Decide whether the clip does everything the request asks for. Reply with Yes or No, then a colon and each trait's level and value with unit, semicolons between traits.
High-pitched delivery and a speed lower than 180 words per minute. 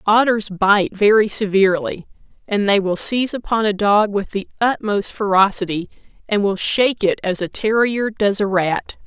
Yes: high, 205 Hz; average, 165 wpm